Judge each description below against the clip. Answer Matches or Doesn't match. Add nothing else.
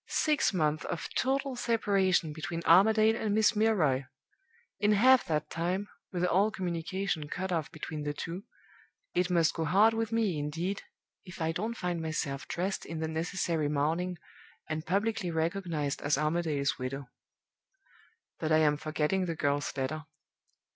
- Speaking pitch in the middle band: Matches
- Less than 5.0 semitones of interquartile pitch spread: Matches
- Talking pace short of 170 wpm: Matches